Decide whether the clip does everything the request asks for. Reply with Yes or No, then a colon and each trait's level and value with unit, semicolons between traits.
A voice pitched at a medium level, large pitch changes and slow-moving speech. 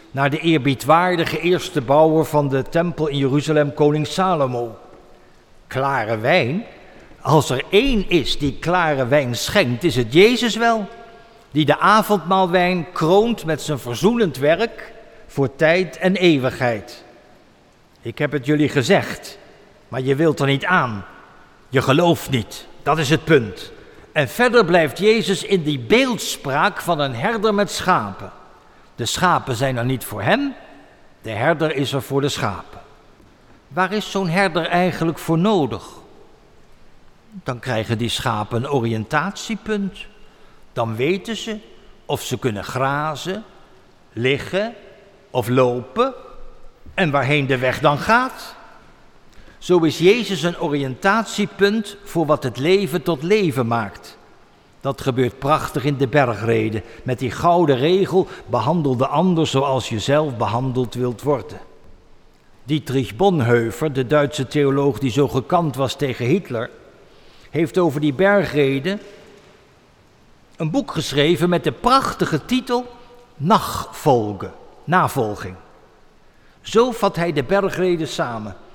Yes: medium, 155 Hz; wide, 6.6 semitones; slow, 130 wpm